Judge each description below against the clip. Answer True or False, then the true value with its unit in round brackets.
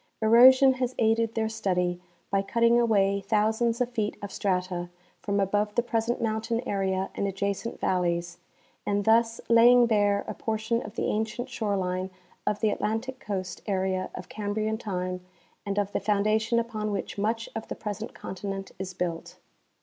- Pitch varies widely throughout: False (2.8 semitones)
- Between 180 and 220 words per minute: False (165 wpm)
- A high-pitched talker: True (210 Hz)